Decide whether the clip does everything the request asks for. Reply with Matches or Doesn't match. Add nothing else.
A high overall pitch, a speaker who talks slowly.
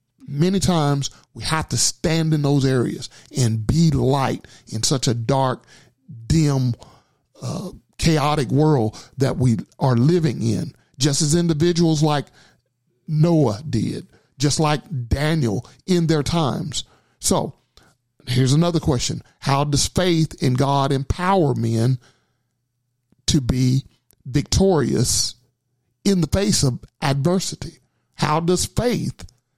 Doesn't match